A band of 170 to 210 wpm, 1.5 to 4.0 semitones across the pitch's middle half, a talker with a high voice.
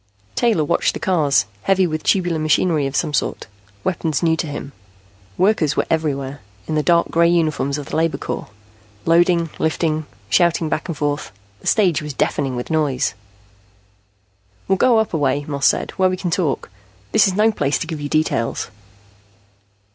No: average, 175 wpm; average, 3.1 semitones; medium, 160 Hz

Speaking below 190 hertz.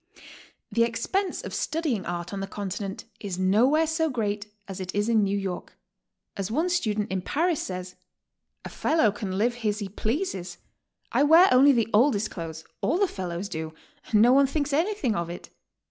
No: high, 210 Hz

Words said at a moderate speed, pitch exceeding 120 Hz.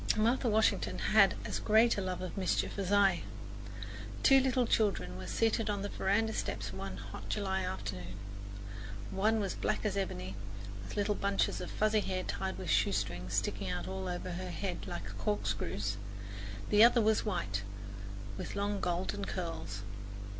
Yes: average, 160 wpm; medium, 185 Hz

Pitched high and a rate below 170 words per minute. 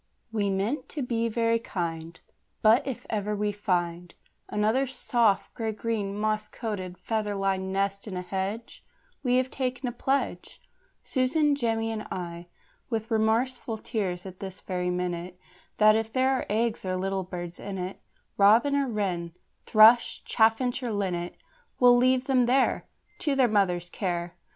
Yes: high, 215 Hz; average, 155 wpm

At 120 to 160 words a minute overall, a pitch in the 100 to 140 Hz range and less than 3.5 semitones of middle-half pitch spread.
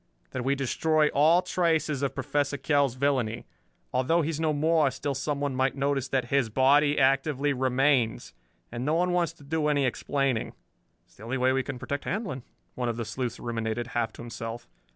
No: average, 190 wpm; low, 135 Hz; average, 2.8 semitones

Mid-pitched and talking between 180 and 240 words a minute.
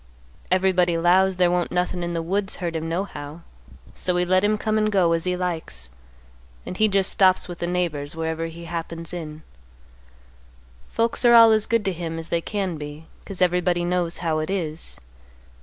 Yes: medium, 175 Hz; average, 190 wpm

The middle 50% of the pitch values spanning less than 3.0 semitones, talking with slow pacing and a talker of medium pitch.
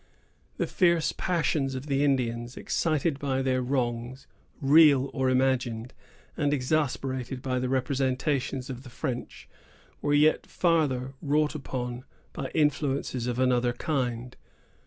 No: narrow, 2.6 semitones; slow, 125 wpm; low, 130 Hz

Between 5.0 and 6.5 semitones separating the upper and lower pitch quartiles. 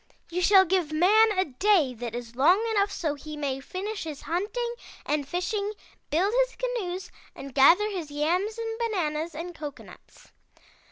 Yes: wide, 5.6 semitones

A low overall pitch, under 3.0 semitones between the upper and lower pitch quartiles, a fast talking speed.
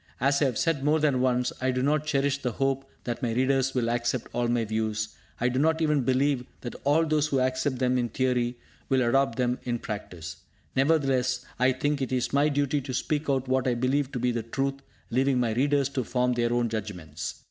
Yes: low, 130 Hz; narrow, 2.5 semitones; fast, 215 wpm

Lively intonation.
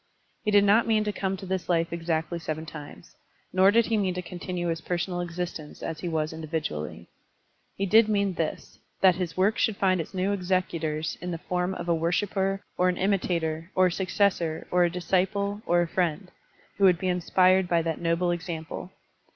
No: narrow, 2.5 semitones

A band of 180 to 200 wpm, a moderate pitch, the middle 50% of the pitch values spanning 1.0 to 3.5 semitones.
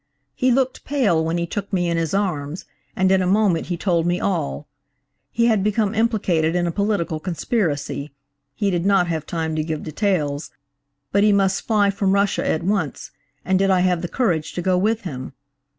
No: average, 185 wpm; medium, 180 Hz; average, 4.3 semitones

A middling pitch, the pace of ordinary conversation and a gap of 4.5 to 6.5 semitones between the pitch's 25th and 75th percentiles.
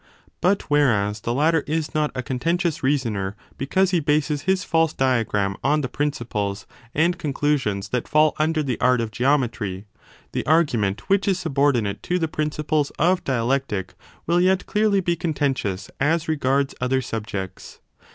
Yes: medium, 145 Hz; average, 155 wpm; wide, 5.5 semitones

